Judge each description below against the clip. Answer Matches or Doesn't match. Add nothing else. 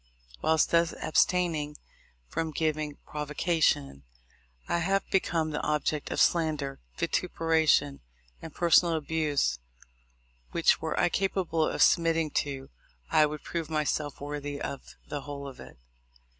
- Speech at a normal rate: Doesn't match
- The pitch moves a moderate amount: Doesn't match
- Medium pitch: Matches